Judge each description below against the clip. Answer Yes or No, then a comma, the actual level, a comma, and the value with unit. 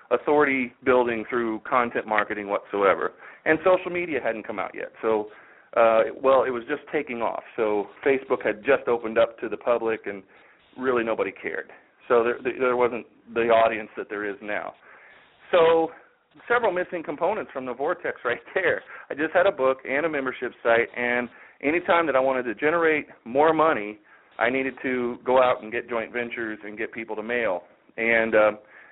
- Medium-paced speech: Yes, average, 180 wpm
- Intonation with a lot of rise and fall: No, average, 3.2 semitones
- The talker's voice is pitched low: Yes, low, 120 Hz